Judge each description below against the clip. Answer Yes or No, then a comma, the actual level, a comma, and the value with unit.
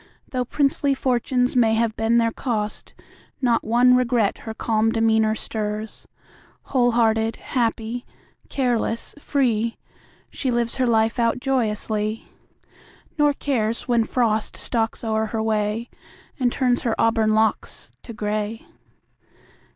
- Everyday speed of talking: No, slow, 125 wpm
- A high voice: Yes, high, 230 Hz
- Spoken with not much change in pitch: Yes, narrow, 2.0 semitones